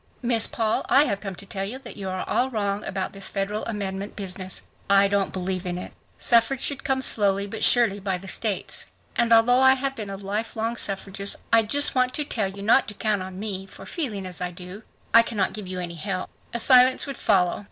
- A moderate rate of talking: No, fast, 225 wpm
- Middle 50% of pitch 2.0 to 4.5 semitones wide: Yes, average, 3.3 semitones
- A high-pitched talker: Yes, high, 205 Hz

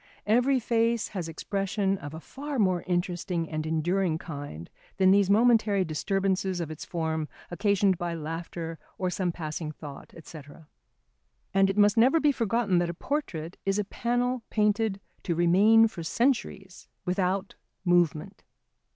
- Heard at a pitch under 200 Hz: Yes, high, 190 Hz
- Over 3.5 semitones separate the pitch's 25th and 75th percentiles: Yes, average, 4.1 semitones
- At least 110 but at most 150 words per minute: Yes, average, 145 wpm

